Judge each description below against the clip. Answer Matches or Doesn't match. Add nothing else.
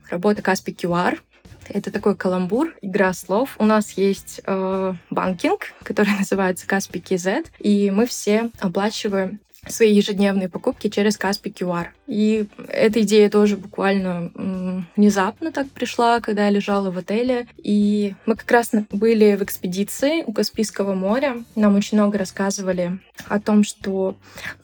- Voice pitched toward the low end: Doesn't match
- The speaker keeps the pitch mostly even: Matches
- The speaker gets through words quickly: Doesn't match